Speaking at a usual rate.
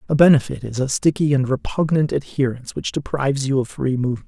Yes: average, 195 wpm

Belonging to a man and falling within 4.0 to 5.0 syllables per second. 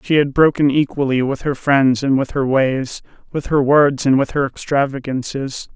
Yes: male; 4.7 syllables/s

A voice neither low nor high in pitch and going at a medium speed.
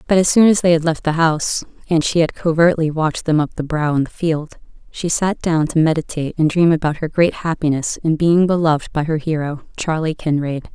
No: medium, 160 Hz; fast, 225 wpm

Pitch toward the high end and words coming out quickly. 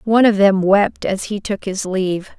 Yes: high, 195 Hz; fast, 225 wpm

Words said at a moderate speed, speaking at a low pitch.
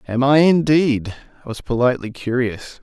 Yes: average, 150 wpm; low, 130 Hz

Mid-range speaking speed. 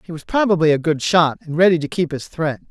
No: fast, 265 wpm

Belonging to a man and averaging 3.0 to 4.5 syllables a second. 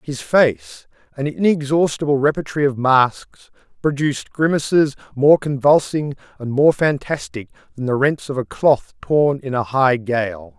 Yes: male; 4.4 syllables/s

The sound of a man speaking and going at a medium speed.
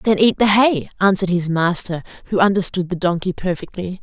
No: female; average, 180 wpm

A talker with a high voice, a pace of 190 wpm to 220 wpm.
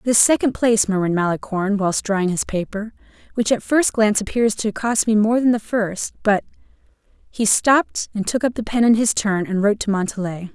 Yes: high, 210 Hz; average, 200 wpm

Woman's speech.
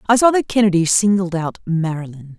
Yes: female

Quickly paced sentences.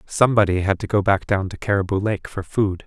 Yes: fast, 230 wpm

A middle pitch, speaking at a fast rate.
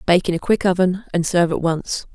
Yes: medium, 180 Hz; fast, 250 wpm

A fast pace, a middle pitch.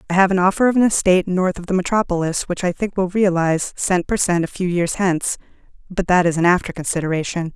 Yes: fast, 230 wpm; medium, 180 Hz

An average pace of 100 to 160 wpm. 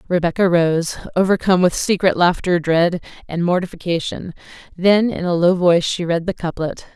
Yes: average, 155 wpm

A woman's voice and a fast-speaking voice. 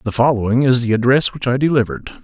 No: male; fast, 215 wpm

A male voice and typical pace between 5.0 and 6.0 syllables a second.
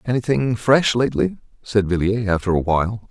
Yes: male; 5.5 syllables/s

